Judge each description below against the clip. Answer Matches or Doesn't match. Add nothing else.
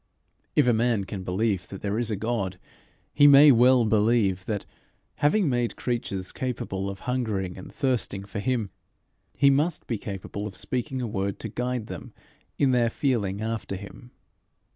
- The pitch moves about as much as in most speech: Matches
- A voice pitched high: Doesn't match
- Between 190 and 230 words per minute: Doesn't match